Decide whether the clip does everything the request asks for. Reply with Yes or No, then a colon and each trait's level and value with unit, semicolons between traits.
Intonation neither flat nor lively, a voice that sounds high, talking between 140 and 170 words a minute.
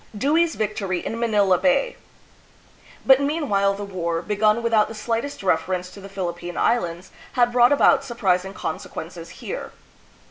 Yes: average, 4.5 semitones; high, 210 Hz; average, 145 wpm